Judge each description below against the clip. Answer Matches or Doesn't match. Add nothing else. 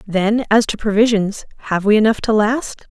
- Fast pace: Doesn't match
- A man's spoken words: Doesn't match